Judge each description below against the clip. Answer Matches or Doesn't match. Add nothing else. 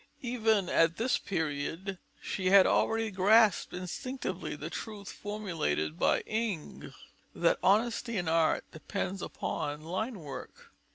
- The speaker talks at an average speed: Doesn't match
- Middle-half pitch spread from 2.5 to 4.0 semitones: Doesn't match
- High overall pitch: Matches